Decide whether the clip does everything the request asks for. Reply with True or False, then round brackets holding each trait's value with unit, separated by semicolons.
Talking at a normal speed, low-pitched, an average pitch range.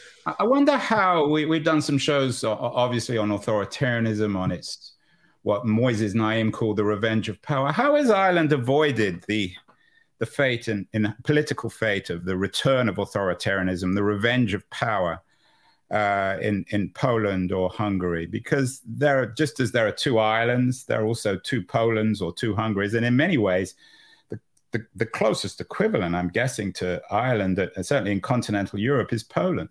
True (170 wpm; 110 Hz; 4.6 semitones)